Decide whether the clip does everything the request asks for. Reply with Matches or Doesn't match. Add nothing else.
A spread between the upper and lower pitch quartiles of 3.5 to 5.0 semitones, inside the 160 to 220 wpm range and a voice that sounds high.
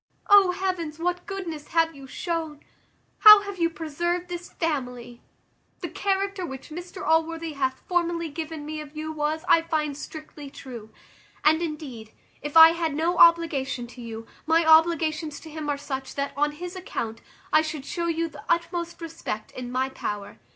Doesn't match